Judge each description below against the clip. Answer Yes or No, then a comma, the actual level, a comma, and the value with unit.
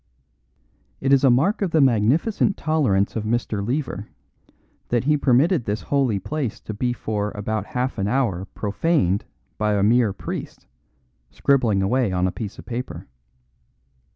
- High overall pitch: No, low, 120 Hz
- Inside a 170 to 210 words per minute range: No, average, 155 wpm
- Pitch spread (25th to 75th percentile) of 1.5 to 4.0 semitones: No, average, 4.9 semitones